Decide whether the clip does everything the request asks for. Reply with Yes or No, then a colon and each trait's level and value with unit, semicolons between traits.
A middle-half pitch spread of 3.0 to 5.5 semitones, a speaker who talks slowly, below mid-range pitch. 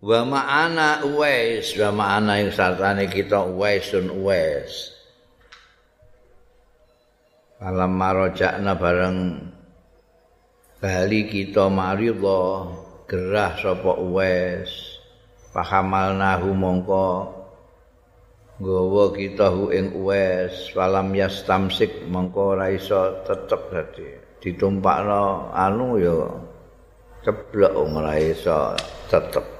Yes: average, 3.8 semitones; slow, 80 wpm; very low, 95 Hz